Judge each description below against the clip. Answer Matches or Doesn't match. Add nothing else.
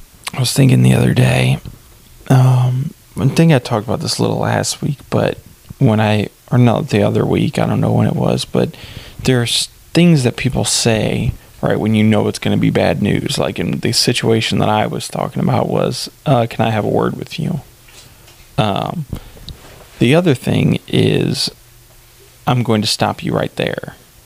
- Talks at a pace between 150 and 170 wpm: Doesn't match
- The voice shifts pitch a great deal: Doesn't match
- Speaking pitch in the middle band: Doesn't match